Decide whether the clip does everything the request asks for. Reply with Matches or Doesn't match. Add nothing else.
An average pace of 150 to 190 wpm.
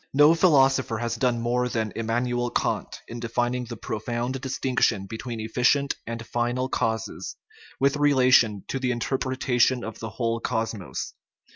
Doesn't match